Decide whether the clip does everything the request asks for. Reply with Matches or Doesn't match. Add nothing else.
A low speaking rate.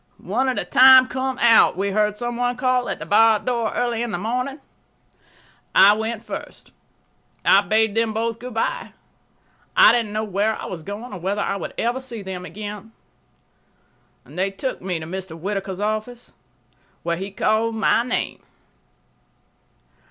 Doesn't match